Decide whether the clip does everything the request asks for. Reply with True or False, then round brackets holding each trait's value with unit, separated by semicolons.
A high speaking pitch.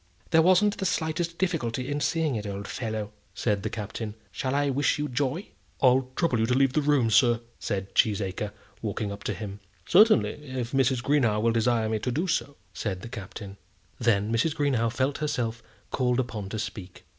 False (120 Hz)